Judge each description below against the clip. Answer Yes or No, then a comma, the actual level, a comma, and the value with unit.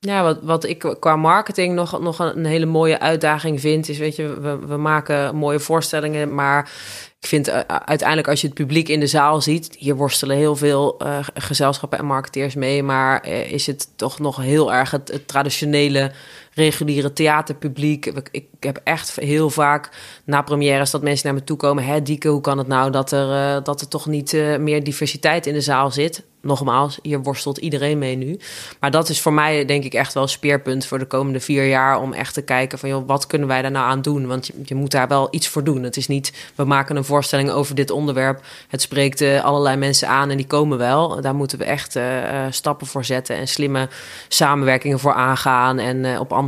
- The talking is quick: Yes, fast, 210 wpm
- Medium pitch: Yes, medium, 145 Hz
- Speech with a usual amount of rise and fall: No, narrow, 1.8 semitones